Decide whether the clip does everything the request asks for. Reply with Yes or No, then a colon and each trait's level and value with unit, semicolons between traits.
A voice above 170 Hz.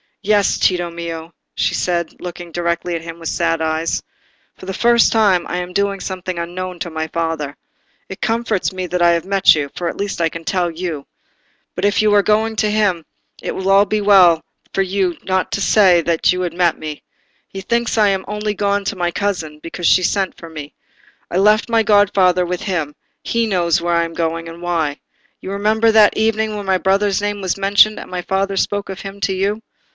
Yes: medium, 185 Hz